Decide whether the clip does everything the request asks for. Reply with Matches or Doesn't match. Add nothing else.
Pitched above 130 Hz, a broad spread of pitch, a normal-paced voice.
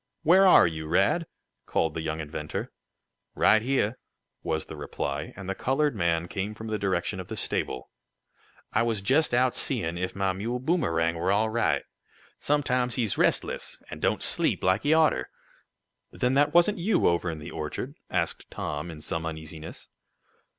Doesn't match